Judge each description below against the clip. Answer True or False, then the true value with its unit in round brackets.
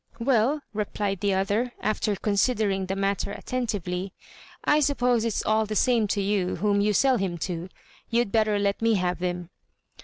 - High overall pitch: True (205 Hz)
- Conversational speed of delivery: True (165 wpm)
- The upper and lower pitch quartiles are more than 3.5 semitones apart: False (2.9 semitones)